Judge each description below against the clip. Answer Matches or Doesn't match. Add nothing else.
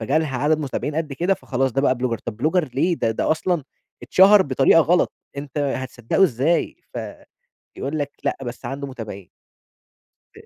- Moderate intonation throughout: Matches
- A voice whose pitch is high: Doesn't match